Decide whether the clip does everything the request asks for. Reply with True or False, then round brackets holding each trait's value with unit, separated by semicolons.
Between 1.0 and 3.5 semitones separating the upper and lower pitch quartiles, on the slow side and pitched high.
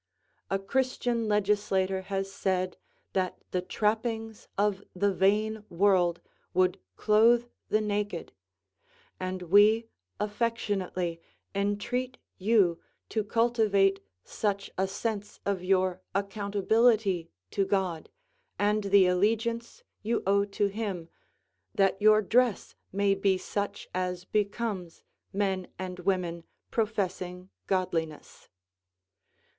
True (2.4 semitones; 105 wpm; 200 Hz)